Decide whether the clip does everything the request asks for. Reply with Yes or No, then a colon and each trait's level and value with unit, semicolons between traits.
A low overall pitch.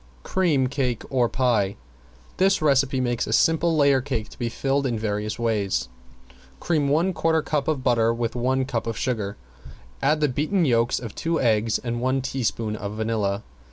Yes: low, 125 Hz